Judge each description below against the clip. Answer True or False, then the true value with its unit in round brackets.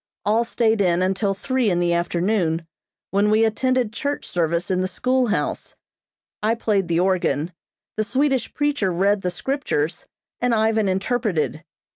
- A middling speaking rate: True (145 wpm)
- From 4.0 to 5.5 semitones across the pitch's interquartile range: True (4.6 semitones)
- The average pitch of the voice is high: True (205 Hz)